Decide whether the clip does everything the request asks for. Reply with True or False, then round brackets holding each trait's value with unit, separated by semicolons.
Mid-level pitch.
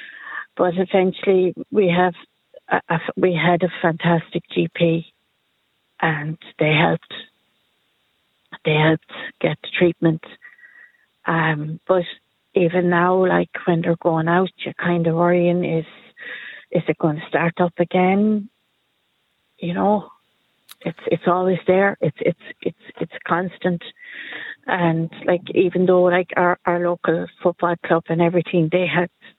True (175 Hz)